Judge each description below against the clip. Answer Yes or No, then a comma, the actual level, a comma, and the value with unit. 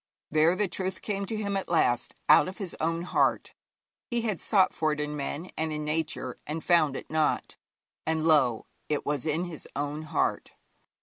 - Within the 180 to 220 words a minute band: Yes, average, 190 wpm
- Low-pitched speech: No, medium, 160 Hz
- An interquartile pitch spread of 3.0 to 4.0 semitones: Yes, average, 3.5 semitones